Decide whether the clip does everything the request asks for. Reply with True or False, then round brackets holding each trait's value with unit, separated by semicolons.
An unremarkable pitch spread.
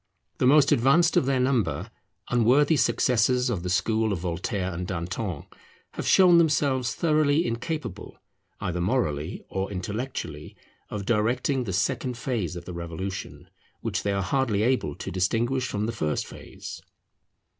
False (6.1 semitones)